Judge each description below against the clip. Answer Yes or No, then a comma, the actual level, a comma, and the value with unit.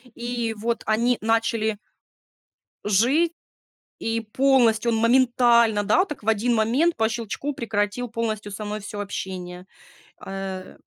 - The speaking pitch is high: Yes, high, 225 Hz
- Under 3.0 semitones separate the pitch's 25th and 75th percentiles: Yes, narrow, 2.5 semitones